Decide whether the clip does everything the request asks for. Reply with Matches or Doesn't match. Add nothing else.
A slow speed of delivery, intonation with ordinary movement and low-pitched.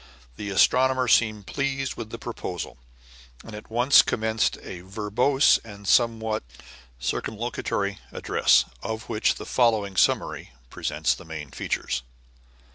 Matches